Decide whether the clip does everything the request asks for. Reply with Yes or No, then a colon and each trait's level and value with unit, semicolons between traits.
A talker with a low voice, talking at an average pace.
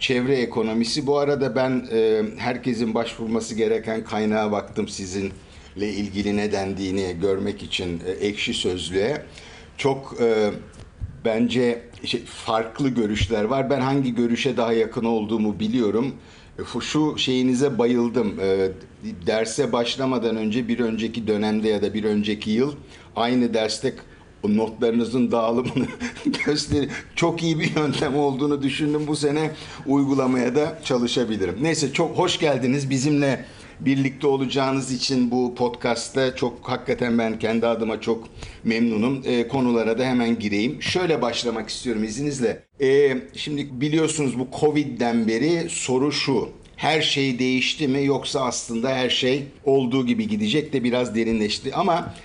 Yes: low, 125 Hz; average, 125 wpm